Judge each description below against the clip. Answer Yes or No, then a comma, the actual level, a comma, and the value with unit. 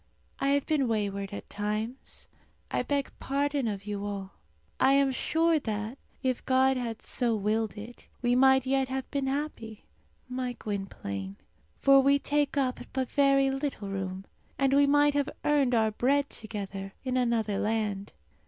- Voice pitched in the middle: No, very high, 250 Hz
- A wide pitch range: No, average, 4.6 semitones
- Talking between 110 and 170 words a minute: Yes, average, 160 wpm